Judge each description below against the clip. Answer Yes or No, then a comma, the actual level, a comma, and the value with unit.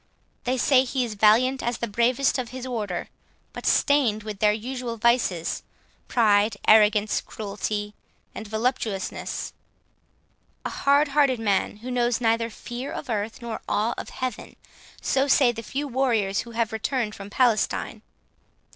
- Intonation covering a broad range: No, average, 3.2 semitones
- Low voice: No, high, 230 Hz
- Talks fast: No, average, 145 wpm